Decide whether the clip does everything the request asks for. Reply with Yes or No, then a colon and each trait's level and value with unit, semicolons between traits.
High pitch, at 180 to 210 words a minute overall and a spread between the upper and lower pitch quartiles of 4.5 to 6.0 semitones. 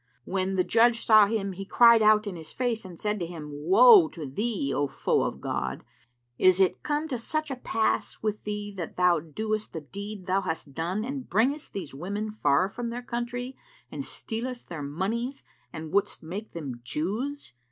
Yes: high, 205 Hz; average, 190 wpm; wide, 5.5 semitones